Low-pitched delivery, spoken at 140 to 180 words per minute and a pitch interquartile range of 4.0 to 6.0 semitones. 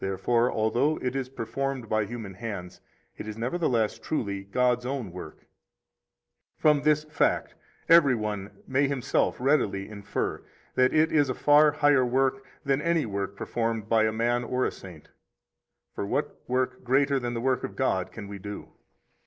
Yes: low, 125 Hz; average, 165 wpm; average, 4.3 semitones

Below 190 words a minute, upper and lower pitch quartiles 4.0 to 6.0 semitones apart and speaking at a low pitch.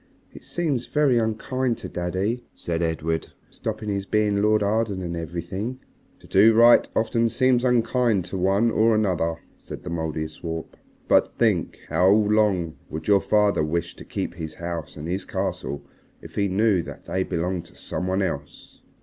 Yes: average, 165 wpm; average, 4.6 semitones; low, 100 Hz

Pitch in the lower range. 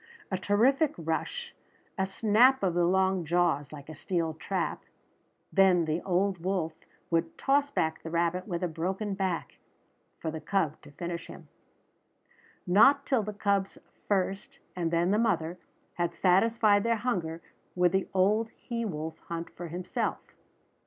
No: medium, 185 Hz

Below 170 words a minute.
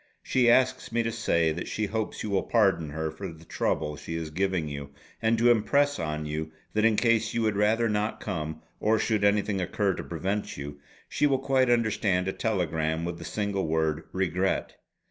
No: average, 200 wpm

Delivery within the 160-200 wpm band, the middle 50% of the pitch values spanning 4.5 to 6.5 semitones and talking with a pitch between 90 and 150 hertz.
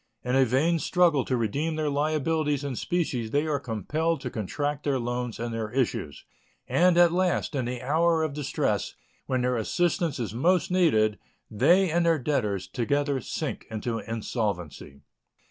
Yes: average, 165 wpm; wide, 5.6 semitones; medium, 140 Hz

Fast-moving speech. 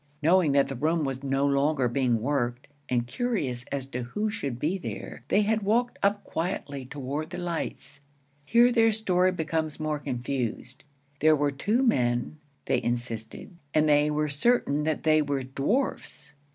No: average, 165 wpm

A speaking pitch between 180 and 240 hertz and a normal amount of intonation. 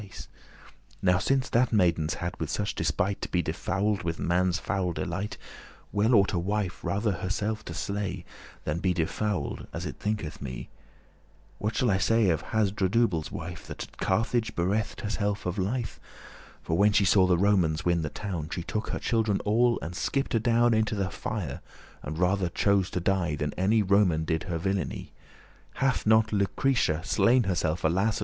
No: very low, 95 Hz; average, 3.6 semitones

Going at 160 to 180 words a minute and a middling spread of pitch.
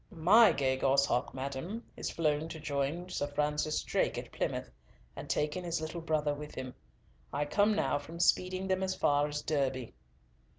Yes: average, 170 wpm; average, 3.5 semitones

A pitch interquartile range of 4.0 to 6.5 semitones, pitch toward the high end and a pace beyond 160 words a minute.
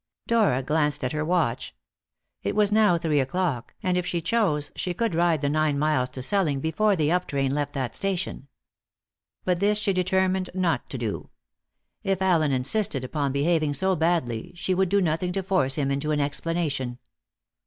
No: average, 4.8 semitones; medium, 165 Hz; average, 180 wpm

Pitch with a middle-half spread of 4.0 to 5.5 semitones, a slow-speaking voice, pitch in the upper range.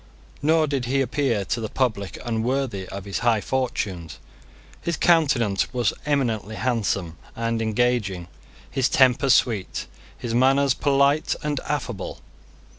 No: average, 4.3 semitones; slow, 125 wpm; low, 120 Hz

